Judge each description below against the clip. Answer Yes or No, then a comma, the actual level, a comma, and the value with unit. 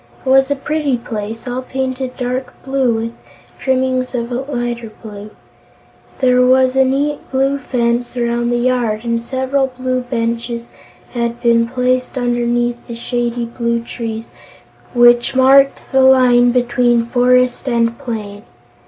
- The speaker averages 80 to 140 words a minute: Yes, slow, 135 wpm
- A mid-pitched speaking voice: No, high, 245 Hz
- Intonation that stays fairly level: Yes, narrow, 1.6 semitones